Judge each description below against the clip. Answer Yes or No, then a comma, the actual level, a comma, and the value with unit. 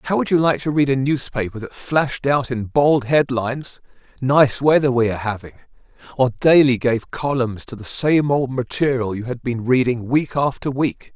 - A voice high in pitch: No, low, 130 Hz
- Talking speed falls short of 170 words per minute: No, average, 190 wpm